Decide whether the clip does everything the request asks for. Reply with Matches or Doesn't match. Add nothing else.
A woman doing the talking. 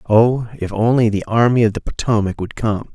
Doesn't match